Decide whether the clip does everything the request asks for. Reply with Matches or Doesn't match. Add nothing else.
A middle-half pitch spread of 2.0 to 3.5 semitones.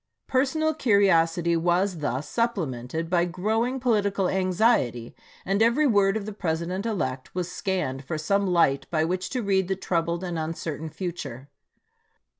Doesn't match